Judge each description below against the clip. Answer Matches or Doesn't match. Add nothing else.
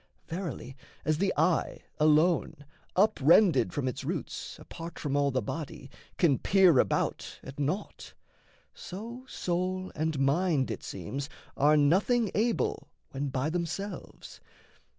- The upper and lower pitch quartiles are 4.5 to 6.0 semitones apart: Matches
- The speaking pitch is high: Doesn't match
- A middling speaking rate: Doesn't match